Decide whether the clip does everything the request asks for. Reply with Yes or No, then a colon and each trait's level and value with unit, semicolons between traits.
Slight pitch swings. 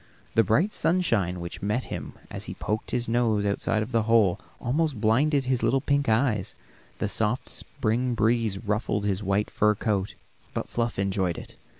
No: average, 3.1 semitones